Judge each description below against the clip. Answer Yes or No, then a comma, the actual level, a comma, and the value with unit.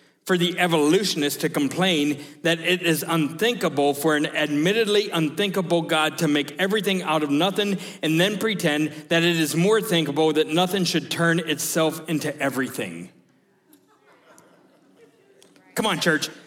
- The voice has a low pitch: No, medium, 165 Hz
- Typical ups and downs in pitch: Yes, average, 3.5 semitones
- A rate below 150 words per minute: Yes, average, 140 wpm